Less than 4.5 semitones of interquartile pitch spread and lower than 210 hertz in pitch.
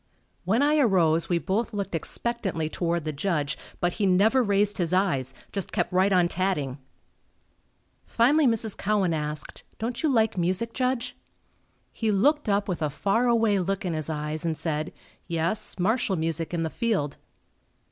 No: wide, 5.4 semitones; high, 190 Hz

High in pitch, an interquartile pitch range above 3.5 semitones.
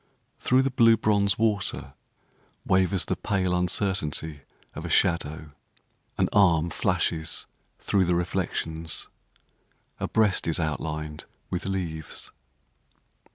No: very low, 90 Hz; average, 3.9 semitones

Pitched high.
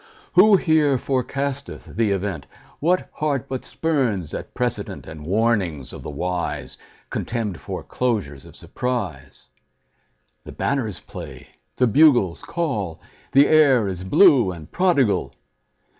No: low, 115 Hz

